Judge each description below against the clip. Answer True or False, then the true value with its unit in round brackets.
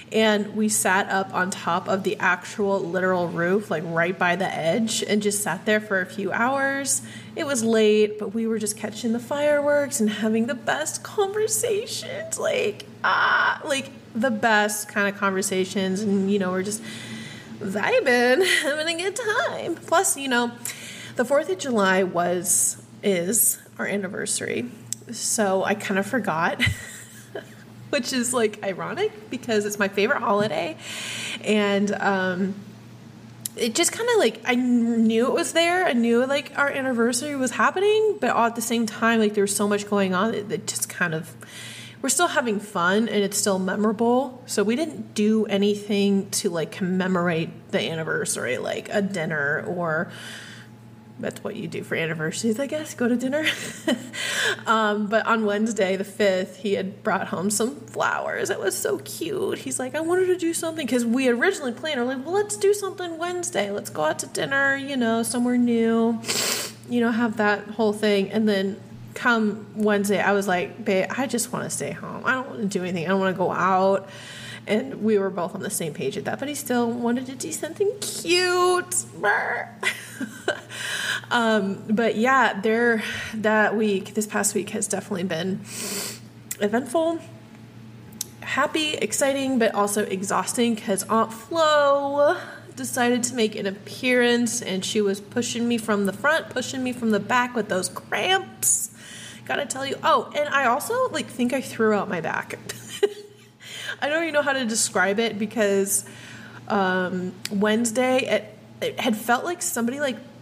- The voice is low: False (215 Hz)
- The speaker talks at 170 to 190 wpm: True (175 wpm)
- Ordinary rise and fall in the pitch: True (4.8 semitones)